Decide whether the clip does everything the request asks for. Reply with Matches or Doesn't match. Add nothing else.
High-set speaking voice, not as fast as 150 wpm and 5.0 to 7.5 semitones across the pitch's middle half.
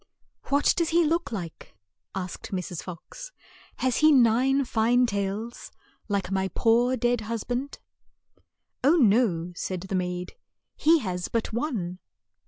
Matches